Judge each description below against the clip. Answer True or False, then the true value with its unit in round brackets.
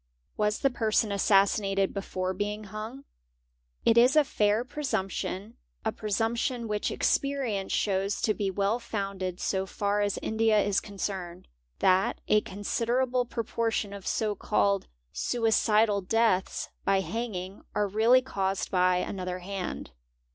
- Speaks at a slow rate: True (125 wpm)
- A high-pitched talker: True (205 Hz)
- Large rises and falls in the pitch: False (2.7 semitones)